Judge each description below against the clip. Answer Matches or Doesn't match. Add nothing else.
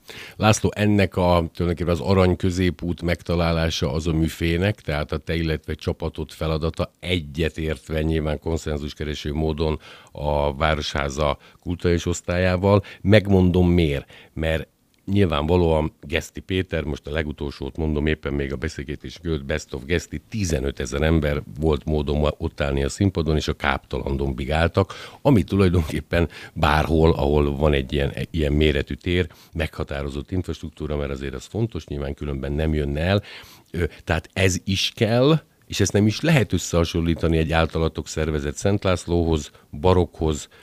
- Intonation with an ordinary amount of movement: Matches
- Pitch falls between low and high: Doesn't match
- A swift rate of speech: Doesn't match